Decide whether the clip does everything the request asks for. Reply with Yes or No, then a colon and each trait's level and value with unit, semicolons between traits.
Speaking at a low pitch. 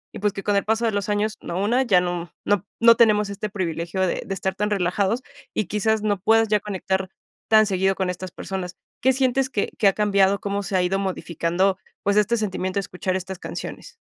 No: high, 200 Hz